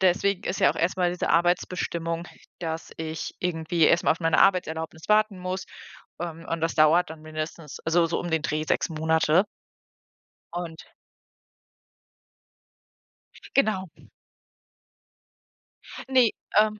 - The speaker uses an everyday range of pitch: No, narrow, 2.1 semitones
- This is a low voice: No, medium, 170 Hz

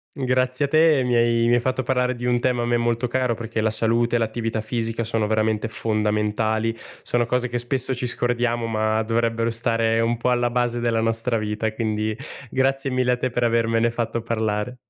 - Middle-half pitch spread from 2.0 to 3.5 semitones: No, narrow, 1.5 semitones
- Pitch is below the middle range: Yes, low, 115 Hz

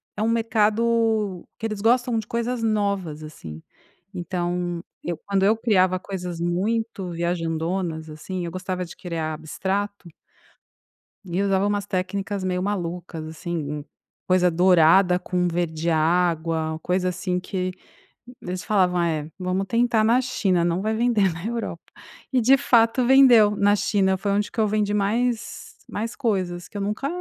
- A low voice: No, high, 190 Hz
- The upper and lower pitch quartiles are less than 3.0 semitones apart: No, average, 3.6 semitones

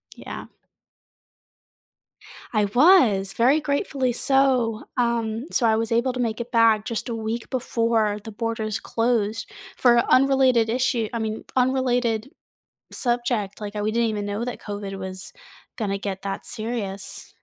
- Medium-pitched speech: No, high, 230 Hz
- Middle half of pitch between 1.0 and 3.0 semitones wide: Yes, narrow, 2.6 semitones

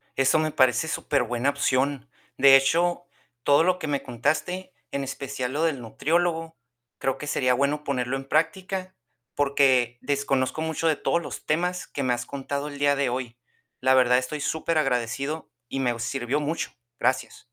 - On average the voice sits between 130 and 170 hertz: Yes, medium, 140 Hz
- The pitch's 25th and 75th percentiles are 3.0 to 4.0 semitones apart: Yes, average, 3.3 semitones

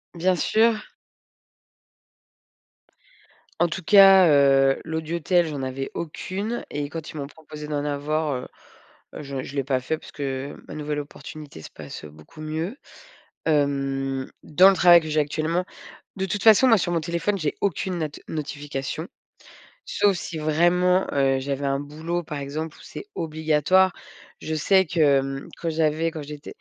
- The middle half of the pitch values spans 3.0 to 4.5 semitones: Yes, average, 3.5 semitones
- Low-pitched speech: No, medium, 155 Hz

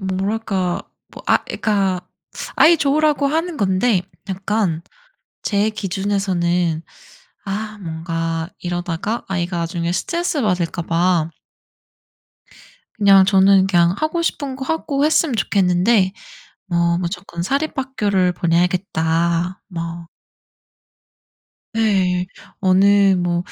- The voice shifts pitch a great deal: No, average, 3.6 semitones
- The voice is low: No, high, 190 Hz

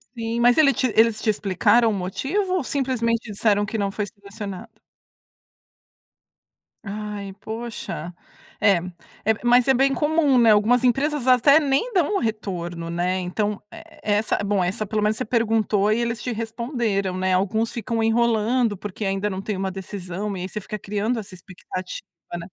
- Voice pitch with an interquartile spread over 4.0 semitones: No, average, 3.3 semitones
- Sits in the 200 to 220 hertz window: Yes, high, 215 Hz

